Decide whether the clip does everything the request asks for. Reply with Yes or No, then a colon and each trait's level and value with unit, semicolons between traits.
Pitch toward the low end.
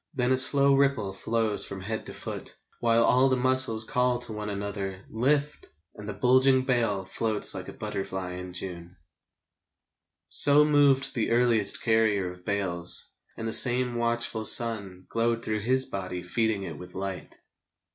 Yes: low, 110 Hz